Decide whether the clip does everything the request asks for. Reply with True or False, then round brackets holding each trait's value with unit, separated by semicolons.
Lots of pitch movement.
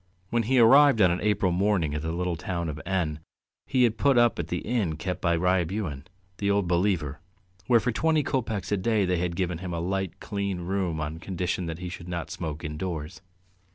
False (3.7 semitones)